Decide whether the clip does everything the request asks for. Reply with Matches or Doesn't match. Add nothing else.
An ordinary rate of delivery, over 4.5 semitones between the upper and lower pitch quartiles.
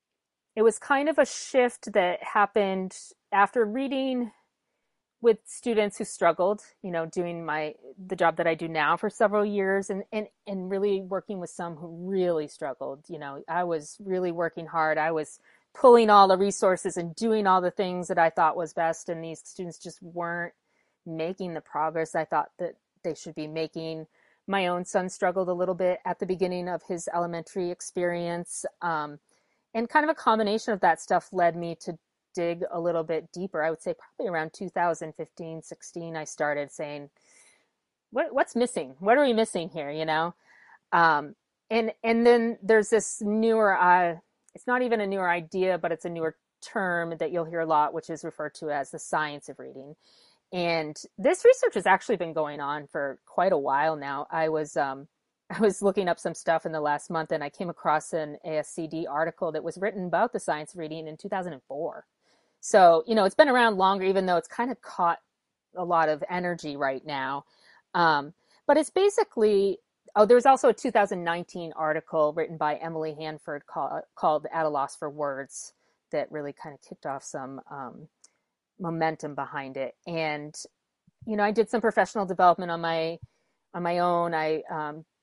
Doesn't match